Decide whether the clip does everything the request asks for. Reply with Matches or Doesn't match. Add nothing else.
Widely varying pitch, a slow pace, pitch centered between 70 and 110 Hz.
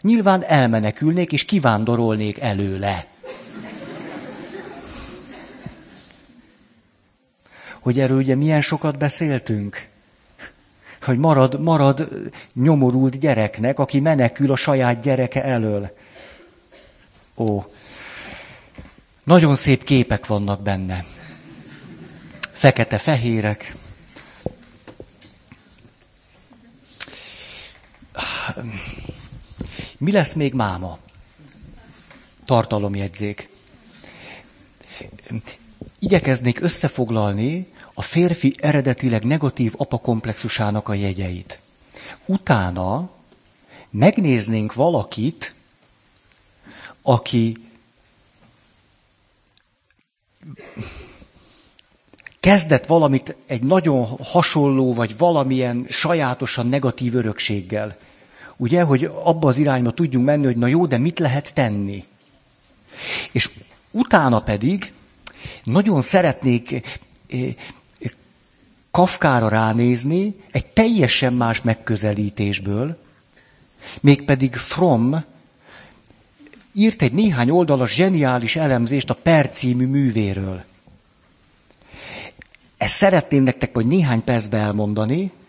Doesn't match